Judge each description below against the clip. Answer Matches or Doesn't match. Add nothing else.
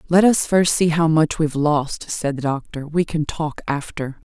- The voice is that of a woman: Matches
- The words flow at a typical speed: Doesn't match